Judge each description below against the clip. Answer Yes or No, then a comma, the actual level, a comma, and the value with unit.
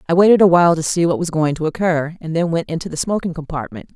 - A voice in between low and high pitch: Yes, medium, 165 Hz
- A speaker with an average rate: No, fast, 260 wpm